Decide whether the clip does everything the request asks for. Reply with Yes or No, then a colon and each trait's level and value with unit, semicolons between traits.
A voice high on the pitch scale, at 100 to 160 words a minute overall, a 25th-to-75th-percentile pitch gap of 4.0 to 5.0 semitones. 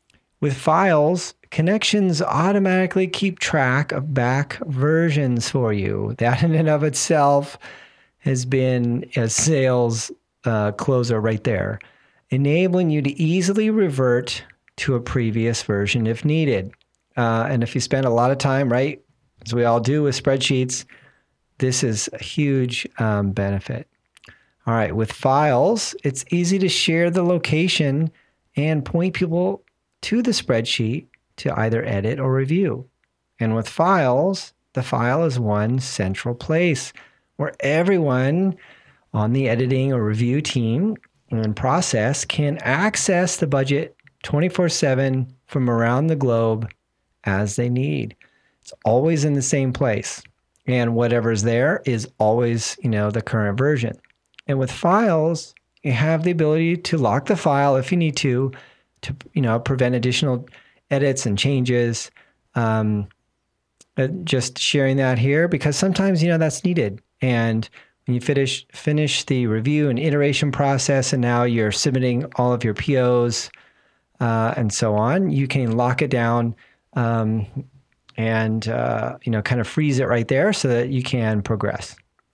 No: low, 130 Hz; average, 145 wpm; average, 4.5 semitones